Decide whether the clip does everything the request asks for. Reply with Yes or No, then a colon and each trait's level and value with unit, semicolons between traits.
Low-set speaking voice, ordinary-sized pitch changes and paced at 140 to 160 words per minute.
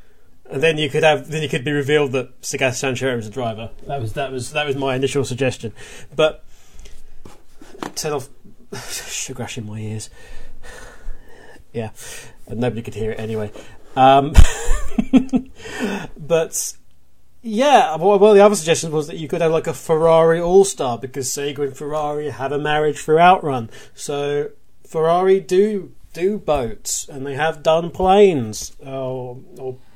No: medium, 145 Hz; average, 4.1 semitones; average, 155 wpm